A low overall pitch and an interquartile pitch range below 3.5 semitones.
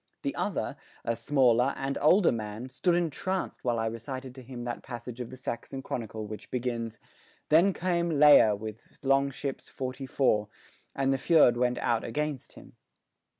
Yes: low, 130 Hz; average, 3.1 semitones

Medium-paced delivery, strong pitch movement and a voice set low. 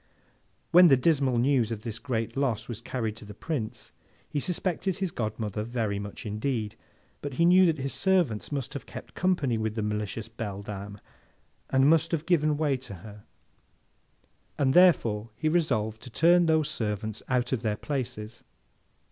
Yes: average, 165 wpm; wide, 6.1 semitones; low, 125 Hz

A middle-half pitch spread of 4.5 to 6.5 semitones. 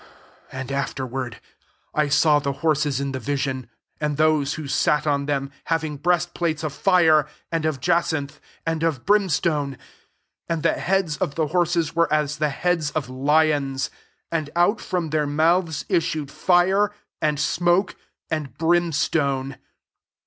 No: average, 3.1 semitones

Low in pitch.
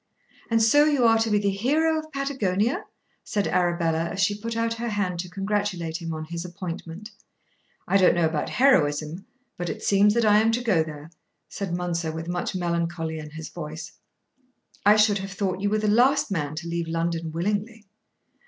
No: high, 190 Hz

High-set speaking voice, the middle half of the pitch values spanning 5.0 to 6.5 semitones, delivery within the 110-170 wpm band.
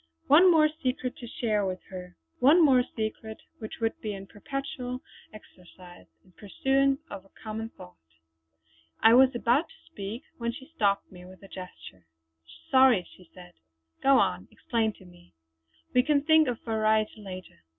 Yes: high, 220 Hz; wide, 5.5 semitones; average, 160 wpm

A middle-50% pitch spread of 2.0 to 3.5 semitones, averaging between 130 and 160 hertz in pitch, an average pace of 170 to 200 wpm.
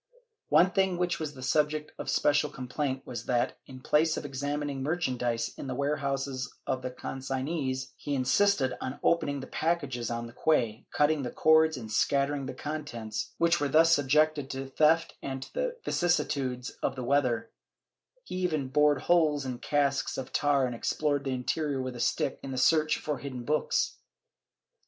Yes: average, 2.9 semitones; medium, 140 Hz; average, 175 wpm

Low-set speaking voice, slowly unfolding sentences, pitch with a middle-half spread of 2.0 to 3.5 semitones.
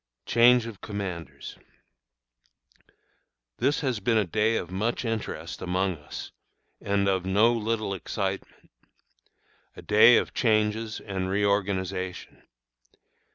Yes: low, 105 Hz; slow, 110 wpm; average, 3.0 semitones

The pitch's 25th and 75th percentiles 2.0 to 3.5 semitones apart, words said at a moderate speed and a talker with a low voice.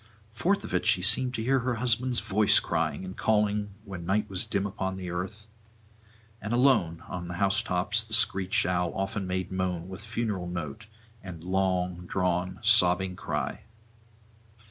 Yes: average, 3.2 semitones; average, 160 wpm; very low, 95 Hz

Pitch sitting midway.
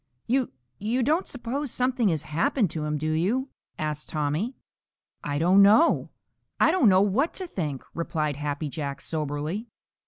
Yes: medium, 180 Hz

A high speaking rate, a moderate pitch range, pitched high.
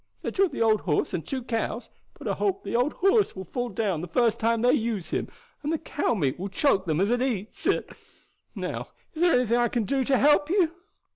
No: fast, 235 wpm; wide, 6.1 semitones; high, 240 Hz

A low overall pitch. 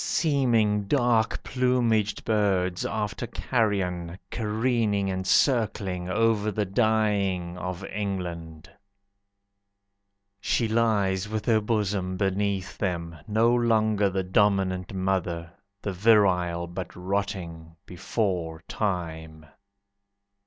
Yes: low, 100 Hz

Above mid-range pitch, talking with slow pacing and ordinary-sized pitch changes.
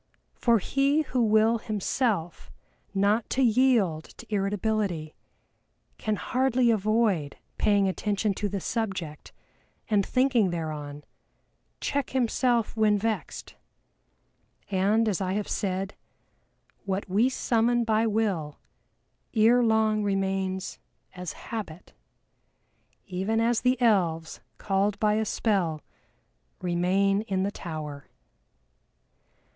Yes: high, 205 Hz; slow, 105 wpm; average, 3.3 semitones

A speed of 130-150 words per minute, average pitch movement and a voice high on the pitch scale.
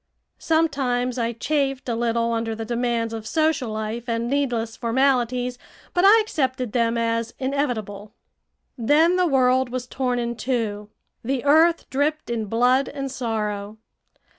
Yes: average, 140 wpm; average, 3.0 semitones; high, 245 Hz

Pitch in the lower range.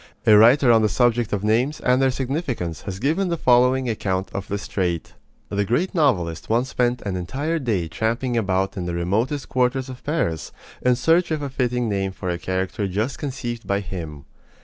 Yes: low, 115 Hz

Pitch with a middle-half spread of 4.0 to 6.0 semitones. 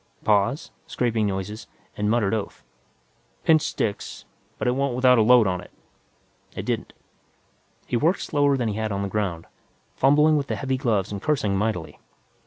Yes: average, 4.8 semitones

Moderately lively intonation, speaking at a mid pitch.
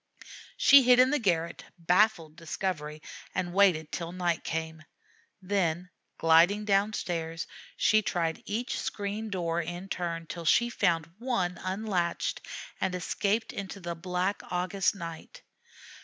Yes: average, 3.3 semitones; medium, 180 Hz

